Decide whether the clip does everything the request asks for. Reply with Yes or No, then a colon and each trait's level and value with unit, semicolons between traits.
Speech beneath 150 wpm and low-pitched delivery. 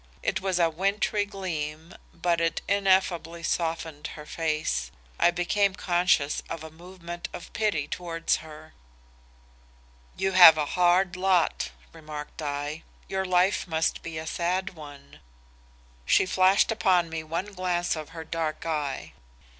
No: average, 140 wpm; medium, 170 Hz